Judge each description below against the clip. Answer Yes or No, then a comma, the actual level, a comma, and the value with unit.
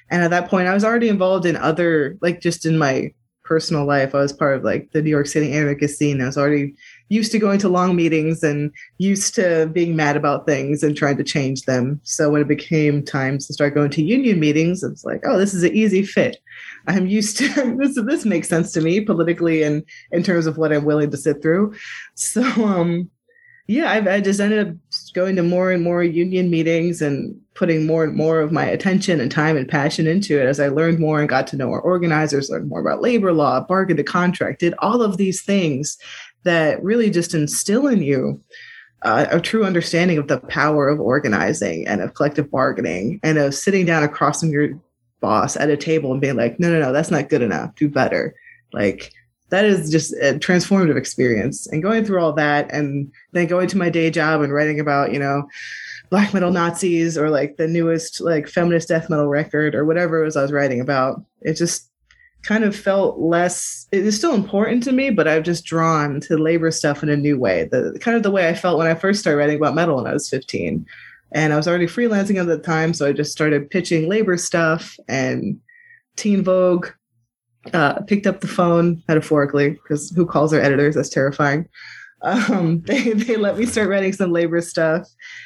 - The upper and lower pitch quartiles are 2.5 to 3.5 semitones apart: No, average, 4.1 semitones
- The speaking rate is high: Yes, fast, 215 wpm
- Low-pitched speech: No, medium, 165 Hz